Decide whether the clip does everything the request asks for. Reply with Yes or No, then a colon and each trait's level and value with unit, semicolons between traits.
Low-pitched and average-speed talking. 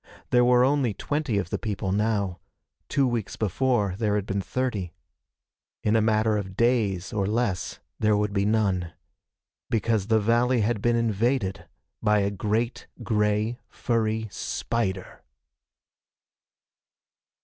No: low, 110 Hz; slow, 130 wpm